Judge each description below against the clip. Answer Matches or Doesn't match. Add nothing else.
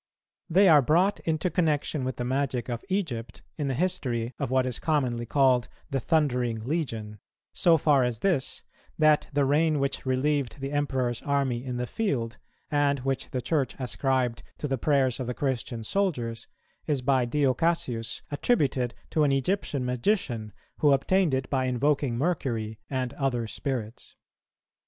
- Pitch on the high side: Doesn't match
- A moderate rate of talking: Matches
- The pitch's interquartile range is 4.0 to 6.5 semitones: Doesn't match